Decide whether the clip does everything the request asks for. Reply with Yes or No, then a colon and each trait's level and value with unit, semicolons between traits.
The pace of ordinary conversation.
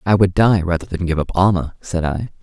No: fast, 250 wpm